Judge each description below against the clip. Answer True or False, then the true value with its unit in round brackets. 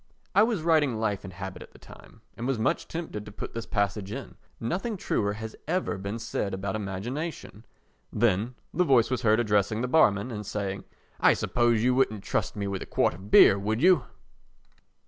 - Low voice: True (110 Hz)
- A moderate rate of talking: True (195 wpm)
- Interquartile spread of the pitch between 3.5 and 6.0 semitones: True (4.2 semitones)